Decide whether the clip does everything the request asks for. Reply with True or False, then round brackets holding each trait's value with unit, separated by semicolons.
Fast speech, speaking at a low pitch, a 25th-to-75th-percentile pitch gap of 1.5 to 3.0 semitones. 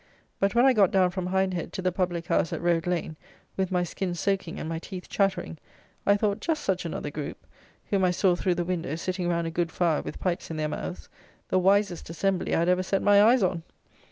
False (230 wpm; 180 Hz; 2.4 semitones)